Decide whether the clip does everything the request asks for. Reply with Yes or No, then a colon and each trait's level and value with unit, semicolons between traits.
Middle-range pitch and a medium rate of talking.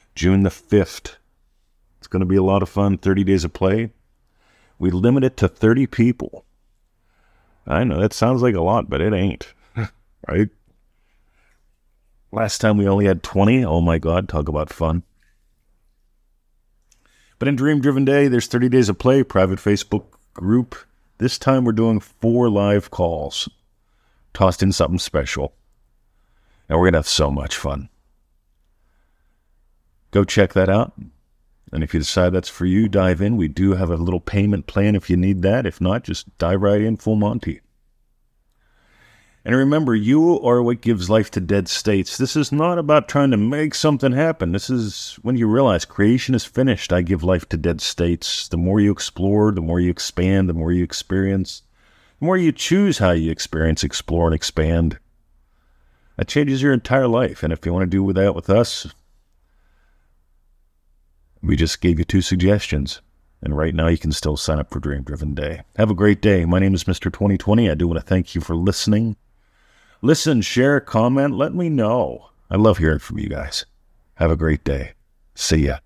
No: very low, 95 Hz; average, 180 wpm